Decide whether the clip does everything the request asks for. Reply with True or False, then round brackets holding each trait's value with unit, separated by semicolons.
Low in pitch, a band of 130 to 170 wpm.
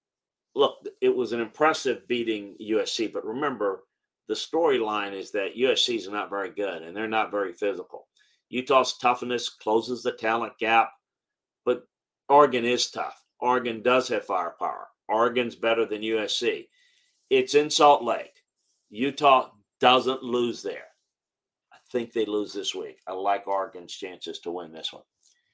True (125 Hz; 150 wpm)